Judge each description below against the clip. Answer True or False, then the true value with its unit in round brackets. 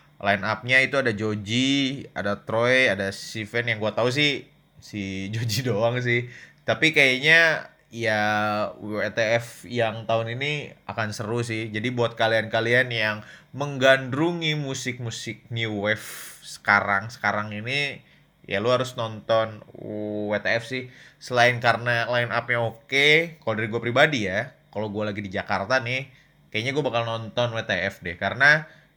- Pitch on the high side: False (115 Hz)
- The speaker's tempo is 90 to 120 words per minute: False (140 wpm)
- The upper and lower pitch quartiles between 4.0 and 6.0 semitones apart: False (3.5 semitones)